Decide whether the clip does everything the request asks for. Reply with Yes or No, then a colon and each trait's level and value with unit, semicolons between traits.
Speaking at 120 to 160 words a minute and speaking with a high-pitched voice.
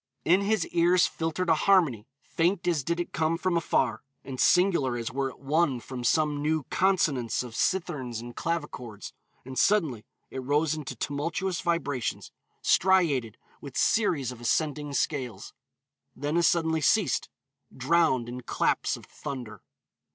No: average, 145 wpm; medium, 150 Hz